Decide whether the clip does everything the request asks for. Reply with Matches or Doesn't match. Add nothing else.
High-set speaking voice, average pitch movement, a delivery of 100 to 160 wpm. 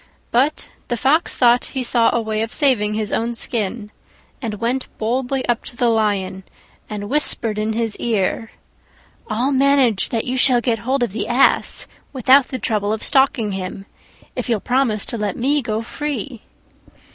Doesn't match